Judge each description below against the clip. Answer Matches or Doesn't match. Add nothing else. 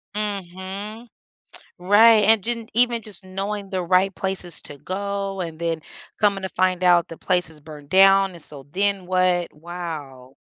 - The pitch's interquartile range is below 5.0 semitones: Matches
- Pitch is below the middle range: Doesn't match